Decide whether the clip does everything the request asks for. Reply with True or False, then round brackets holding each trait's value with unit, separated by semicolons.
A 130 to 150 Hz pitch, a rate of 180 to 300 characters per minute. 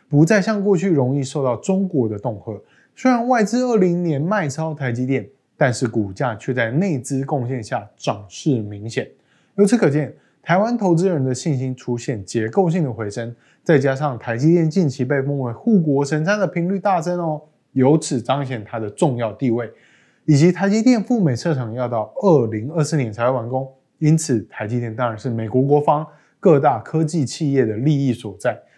True (140 Hz; 280 characters per minute)